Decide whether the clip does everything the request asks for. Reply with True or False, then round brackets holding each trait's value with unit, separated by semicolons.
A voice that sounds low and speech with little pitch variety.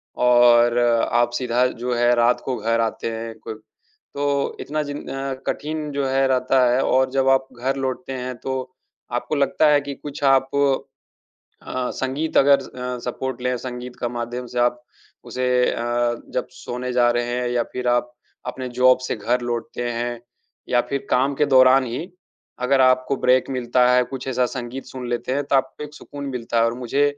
True (125 Hz; 1.8 semitones)